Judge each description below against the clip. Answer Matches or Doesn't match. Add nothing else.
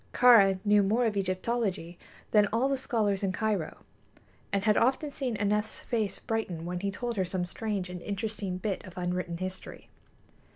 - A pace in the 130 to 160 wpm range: Doesn't match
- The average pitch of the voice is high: Matches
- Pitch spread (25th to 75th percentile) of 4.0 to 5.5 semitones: Doesn't match